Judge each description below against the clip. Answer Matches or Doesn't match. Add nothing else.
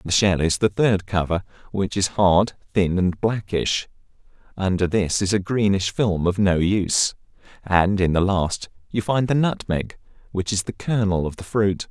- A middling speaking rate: Matches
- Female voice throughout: Doesn't match